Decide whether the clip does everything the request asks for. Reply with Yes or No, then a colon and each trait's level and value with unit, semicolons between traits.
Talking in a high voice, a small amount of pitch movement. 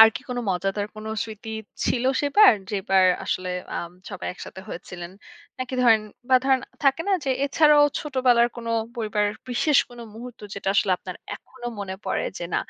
No: high, 230 Hz; average, 4.9 semitones